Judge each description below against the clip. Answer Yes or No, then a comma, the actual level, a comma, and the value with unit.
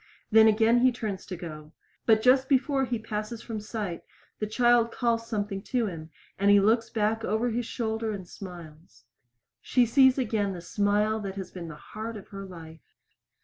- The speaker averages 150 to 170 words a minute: No, average, 185 wpm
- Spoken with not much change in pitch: No, average, 3.1 semitones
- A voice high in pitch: Yes, high, 215 Hz